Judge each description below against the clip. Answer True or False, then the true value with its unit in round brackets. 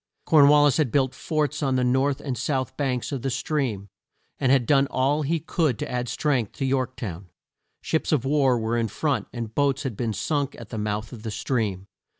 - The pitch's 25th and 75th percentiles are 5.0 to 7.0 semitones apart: False (3.7 semitones)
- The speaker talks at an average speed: False (215 wpm)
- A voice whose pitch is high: False (130 Hz)